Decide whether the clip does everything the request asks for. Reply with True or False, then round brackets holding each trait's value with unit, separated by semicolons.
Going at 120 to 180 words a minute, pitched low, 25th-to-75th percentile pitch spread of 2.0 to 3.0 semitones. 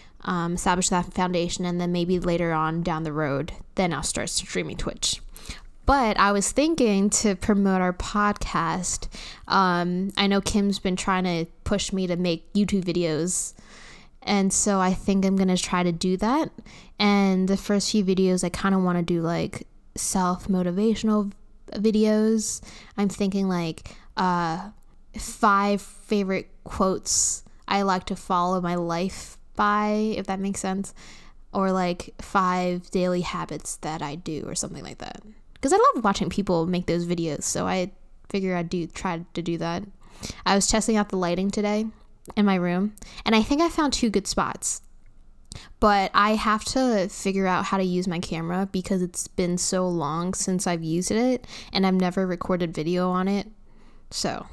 False (175 wpm; 190 Hz; 2.4 semitones)